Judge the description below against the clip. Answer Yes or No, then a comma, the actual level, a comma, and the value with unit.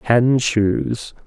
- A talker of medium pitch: No, low, 115 Hz